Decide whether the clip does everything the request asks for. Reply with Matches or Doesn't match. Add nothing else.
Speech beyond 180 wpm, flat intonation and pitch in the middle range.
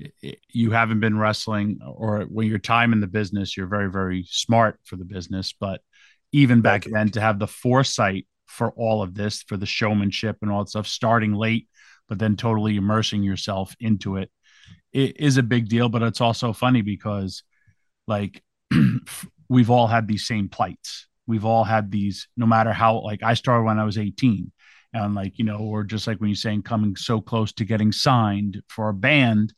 Doesn't match